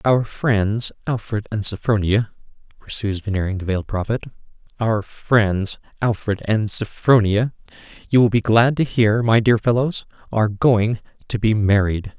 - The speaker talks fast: No, average, 145 wpm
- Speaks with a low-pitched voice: Yes, low, 110 Hz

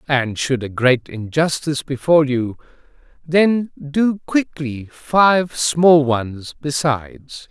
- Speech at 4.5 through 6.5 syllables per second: No, 3.2 syllables/s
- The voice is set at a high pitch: No, medium, 145 Hz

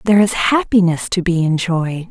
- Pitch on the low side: No, medium, 180 Hz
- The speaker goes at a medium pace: Yes, average, 170 wpm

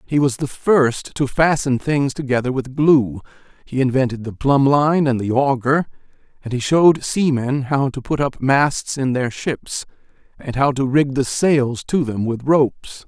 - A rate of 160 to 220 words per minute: Yes, average, 185 wpm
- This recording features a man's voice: Yes, male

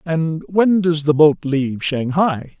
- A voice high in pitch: No, medium, 160 Hz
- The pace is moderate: Yes, average, 160 wpm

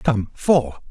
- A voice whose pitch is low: Yes, low, 120 Hz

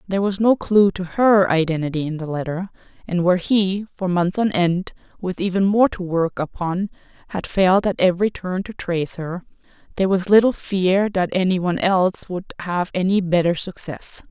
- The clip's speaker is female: Yes, female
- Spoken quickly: No, average, 185 wpm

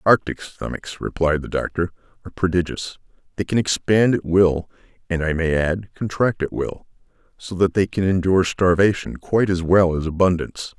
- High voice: No, very low, 90 Hz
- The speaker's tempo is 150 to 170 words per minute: Yes, average, 165 wpm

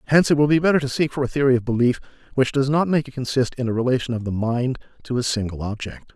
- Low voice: Yes, low, 130 Hz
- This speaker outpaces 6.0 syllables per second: Yes, 7.0 syllables/s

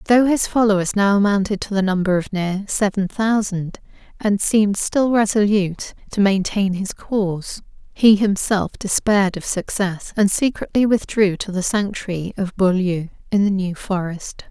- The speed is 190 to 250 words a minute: No, average, 155 wpm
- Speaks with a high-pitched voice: Yes, high, 200 Hz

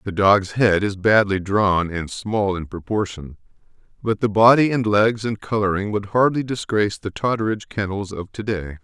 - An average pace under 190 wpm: Yes, average, 175 wpm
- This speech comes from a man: Yes, male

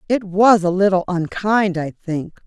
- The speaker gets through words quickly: No, average, 170 wpm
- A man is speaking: No, female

